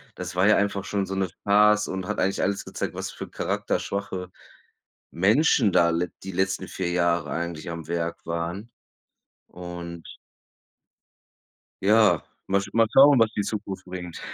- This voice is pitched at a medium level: No, very low, 95 Hz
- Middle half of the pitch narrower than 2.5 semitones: No, average, 2.8 semitones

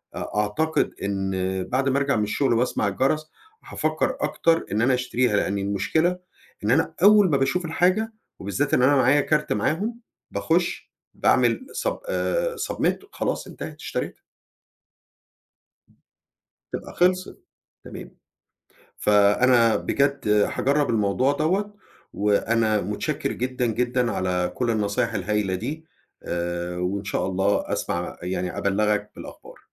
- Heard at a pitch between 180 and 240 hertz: No, low, 115 Hz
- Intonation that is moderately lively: No, wide, 6.3 semitones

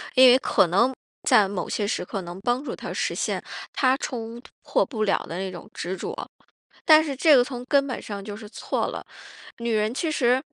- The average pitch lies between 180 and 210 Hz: No, high, 235 Hz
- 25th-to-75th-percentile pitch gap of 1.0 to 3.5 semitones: No, average, 4.5 semitones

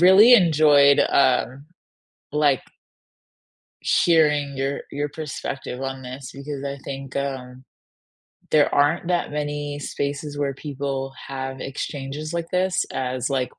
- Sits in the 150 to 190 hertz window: No, medium, 140 Hz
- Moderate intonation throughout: No, narrow, 1.8 semitones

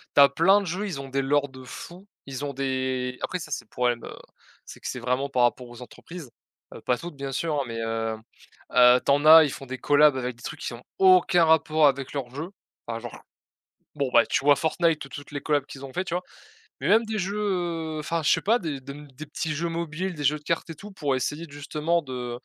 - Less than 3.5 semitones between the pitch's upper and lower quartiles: No, average, 4.1 semitones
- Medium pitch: Yes, medium, 145 Hz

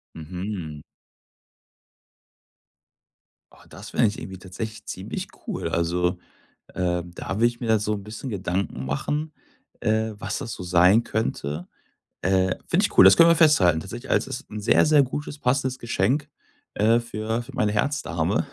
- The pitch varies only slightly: No, average, 4.7 semitones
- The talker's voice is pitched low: Yes, low, 105 Hz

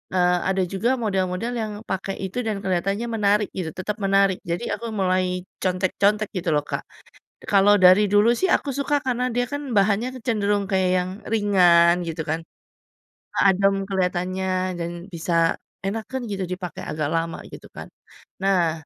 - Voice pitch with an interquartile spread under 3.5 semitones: Yes, average, 2.8 semitones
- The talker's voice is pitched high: Yes, high, 195 Hz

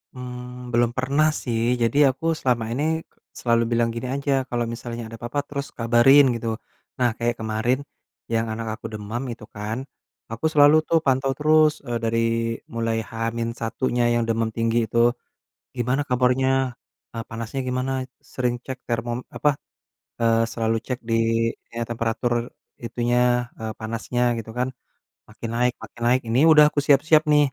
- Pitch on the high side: No, low, 120 Hz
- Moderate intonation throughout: No, narrow, 2.1 semitones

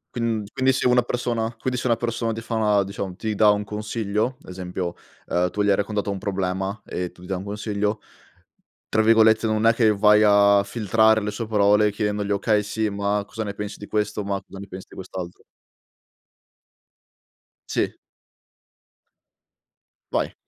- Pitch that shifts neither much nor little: No, narrow, 1.8 semitones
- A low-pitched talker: Yes, low, 105 Hz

